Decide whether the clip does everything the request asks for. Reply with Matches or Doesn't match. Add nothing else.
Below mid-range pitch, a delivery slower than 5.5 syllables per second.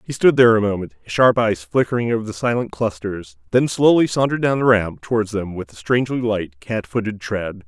Doesn't match